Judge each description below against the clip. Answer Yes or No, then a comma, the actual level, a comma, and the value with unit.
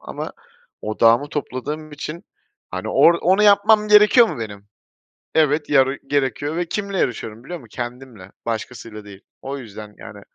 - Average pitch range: No, wide, 7.0 semitones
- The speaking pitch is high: No, low, 135 Hz